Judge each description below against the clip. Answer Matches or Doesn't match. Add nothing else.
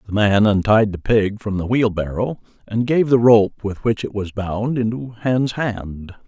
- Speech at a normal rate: Matches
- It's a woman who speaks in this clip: Doesn't match